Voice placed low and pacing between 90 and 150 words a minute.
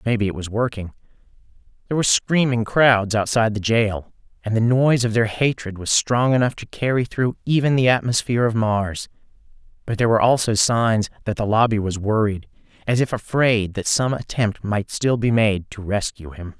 No: low, 110 Hz; average, 185 wpm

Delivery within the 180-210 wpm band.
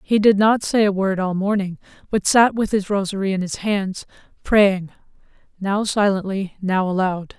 No: average, 170 wpm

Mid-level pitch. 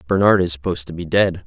No: very low, 90 Hz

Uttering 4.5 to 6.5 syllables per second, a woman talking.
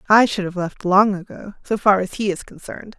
Yes: 5.5 syllables/s; female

